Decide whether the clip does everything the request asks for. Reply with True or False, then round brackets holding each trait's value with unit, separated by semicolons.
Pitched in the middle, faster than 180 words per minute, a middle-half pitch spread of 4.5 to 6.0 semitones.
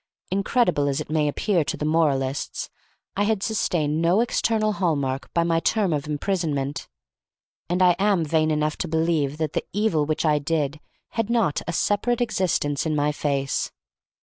False (160 Hz; 170 wpm; 4.8 semitones)